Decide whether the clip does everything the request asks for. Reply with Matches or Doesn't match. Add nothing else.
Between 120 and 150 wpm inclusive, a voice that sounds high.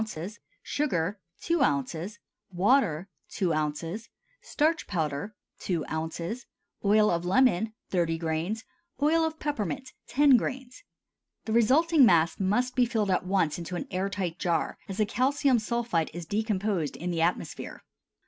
Matches